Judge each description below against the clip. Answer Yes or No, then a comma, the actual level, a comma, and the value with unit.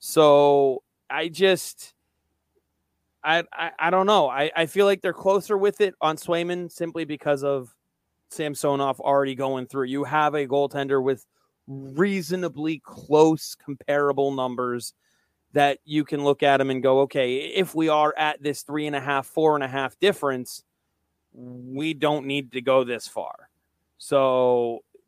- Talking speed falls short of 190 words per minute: Yes, average, 155 wpm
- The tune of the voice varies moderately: Yes, average, 3.0 semitones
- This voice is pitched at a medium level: Yes, medium, 145 Hz